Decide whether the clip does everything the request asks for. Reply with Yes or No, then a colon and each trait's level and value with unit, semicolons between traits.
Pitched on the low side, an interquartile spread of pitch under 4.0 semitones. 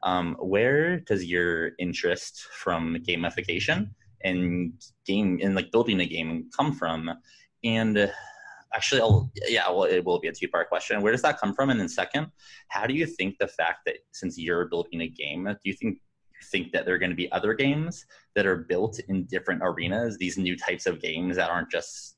No: very low, 95 Hz; average, 5.3 semitones